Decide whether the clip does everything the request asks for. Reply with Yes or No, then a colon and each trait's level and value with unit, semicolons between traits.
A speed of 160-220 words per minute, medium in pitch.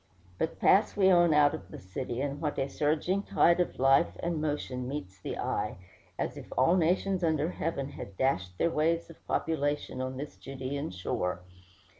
Yes: average, 180 wpm; medium, 145 Hz